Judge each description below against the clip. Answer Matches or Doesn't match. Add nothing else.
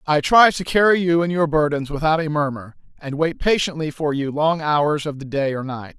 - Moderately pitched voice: Matches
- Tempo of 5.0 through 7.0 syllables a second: Matches